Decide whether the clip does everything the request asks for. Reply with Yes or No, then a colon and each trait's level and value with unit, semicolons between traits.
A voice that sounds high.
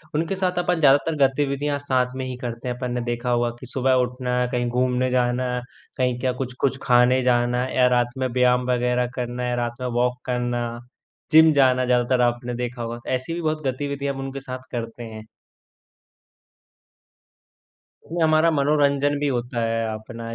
No: low, 125 Hz